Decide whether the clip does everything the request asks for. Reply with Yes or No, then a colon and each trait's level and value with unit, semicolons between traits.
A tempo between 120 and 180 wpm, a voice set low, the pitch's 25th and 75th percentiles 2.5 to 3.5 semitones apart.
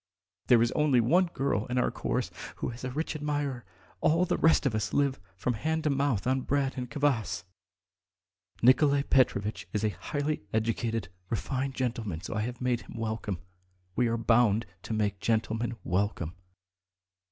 No: average, 165 wpm; low, 120 Hz; average, 4.1 semitones